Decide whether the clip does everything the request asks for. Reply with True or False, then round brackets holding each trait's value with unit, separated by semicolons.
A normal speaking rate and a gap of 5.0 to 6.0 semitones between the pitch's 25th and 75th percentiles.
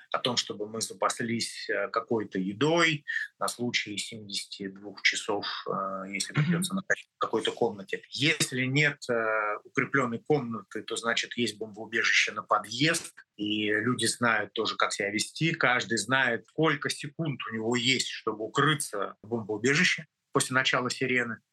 True (135 wpm; 5.5 semitones)